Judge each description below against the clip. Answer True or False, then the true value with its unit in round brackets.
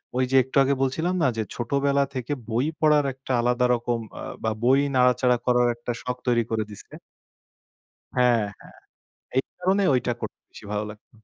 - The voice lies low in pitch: True (125 Hz)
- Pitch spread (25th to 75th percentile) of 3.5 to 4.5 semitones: False (2.4 semitones)